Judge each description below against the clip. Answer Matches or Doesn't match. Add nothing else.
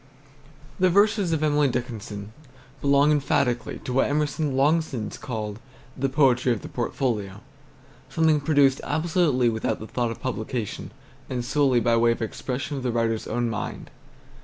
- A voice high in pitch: Doesn't match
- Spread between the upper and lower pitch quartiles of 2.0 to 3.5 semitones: Doesn't match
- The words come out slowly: Doesn't match